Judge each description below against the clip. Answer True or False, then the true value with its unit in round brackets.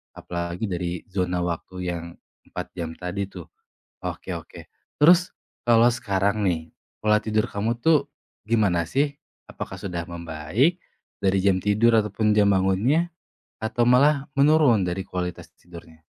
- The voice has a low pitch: True (100 Hz)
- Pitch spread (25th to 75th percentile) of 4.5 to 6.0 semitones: True (5.0 semitones)